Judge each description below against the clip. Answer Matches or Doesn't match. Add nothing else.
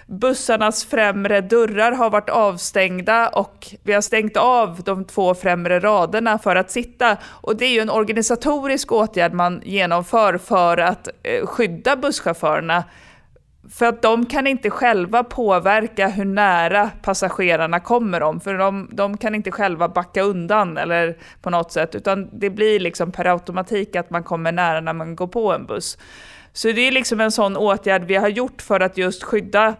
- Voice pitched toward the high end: Matches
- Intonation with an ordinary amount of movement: Matches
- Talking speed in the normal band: Matches